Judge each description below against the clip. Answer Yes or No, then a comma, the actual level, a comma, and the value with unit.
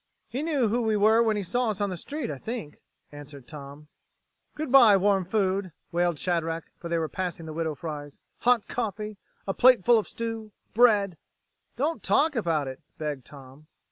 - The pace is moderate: Yes, average, 185 wpm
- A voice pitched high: Yes, high, 195 Hz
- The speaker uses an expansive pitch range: Yes, wide, 6.5 semitones